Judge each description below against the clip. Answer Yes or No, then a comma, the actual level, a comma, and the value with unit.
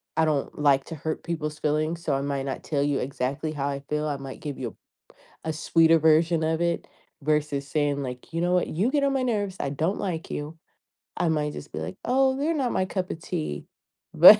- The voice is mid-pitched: Yes, medium, 155 Hz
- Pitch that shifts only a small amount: No, average, 3.2 semitones